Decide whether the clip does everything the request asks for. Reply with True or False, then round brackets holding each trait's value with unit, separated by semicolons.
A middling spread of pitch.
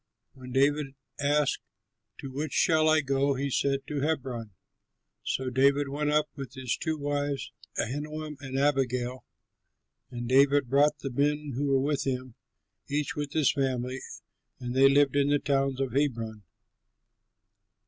False (1.8 semitones)